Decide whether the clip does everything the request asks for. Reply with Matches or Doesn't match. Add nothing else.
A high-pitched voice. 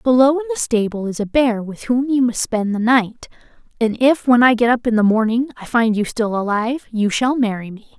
Matches